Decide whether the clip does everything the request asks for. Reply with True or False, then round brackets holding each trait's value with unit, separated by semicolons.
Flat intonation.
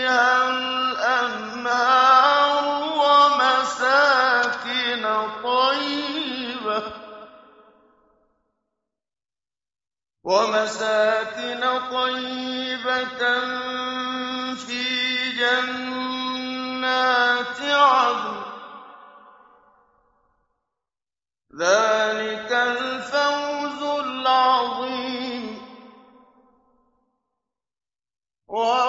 True (0.8 semitones)